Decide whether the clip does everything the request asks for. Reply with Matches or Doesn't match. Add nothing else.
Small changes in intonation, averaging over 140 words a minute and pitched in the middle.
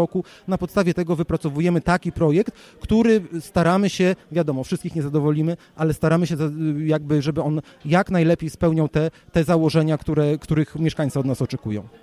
Matches